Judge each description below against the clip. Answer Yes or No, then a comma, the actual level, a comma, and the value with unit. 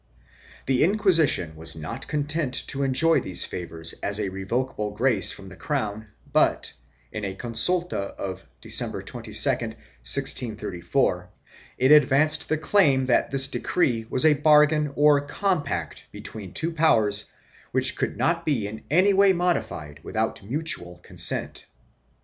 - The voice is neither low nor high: No, low, 130 Hz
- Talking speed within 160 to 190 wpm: No, average, 140 wpm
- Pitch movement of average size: No, wide, 7.4 semitones